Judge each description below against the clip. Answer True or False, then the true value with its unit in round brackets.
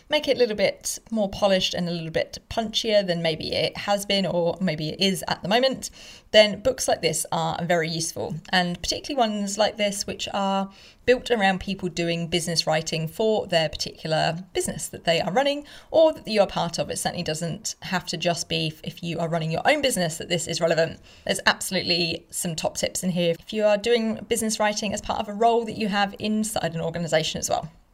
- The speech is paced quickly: True (220 wpm)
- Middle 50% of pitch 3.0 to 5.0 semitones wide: True (4.2 semitones)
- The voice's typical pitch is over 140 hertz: True (185 Hz)